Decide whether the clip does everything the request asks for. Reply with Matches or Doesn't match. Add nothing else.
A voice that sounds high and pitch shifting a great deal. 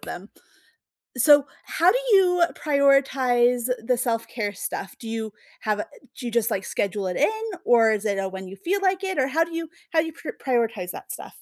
Matches